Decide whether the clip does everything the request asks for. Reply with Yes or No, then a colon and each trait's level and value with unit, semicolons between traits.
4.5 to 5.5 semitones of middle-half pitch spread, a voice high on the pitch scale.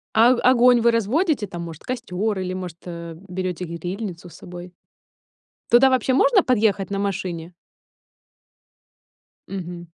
Yes: average, 5.2 semitones; high, 195 Hz